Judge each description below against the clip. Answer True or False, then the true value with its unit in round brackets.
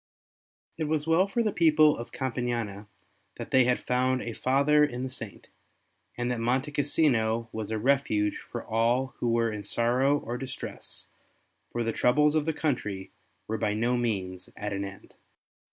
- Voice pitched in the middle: False (125 Hz)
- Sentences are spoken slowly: False (170 wpm)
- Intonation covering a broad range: False (4.1 semitones)